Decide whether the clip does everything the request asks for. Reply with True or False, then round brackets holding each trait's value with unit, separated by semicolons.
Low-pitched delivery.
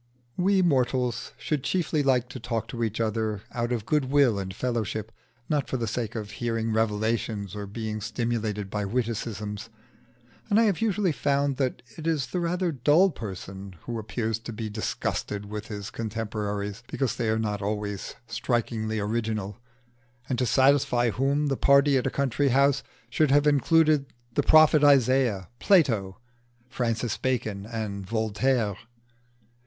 True (115 Hz)